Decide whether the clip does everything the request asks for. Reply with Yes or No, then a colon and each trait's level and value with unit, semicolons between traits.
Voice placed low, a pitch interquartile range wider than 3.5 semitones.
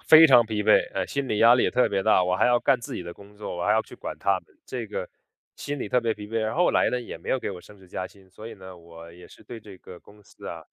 Yes: low, 105 Hz; average, 4.1 semitones